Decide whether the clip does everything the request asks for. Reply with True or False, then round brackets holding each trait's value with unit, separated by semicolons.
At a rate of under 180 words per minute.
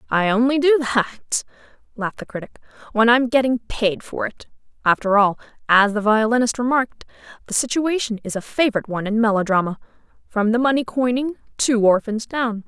True (160 wpm)